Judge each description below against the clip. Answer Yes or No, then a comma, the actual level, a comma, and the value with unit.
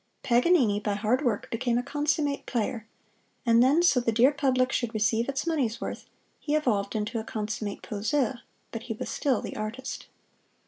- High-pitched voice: Yes, high, 240 Hz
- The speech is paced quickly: No, average, 175 wpm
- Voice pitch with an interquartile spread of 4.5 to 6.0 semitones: No, average, 4.0 semitones